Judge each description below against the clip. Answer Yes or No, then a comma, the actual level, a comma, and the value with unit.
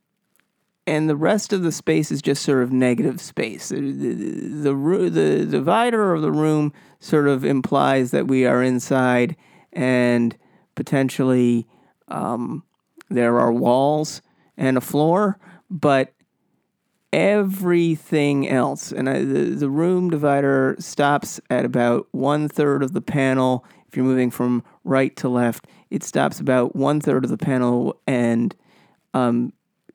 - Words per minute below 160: Yes, average, 140 wpm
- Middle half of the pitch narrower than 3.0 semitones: No, average, 4.1 semitones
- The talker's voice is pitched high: No, medium, 140 Hz